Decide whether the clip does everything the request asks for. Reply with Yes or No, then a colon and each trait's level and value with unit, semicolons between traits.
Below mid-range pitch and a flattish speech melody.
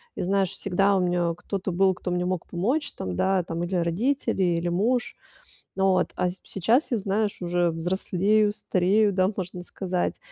No: medium, 185 Hz; narrow, 2.3 semitones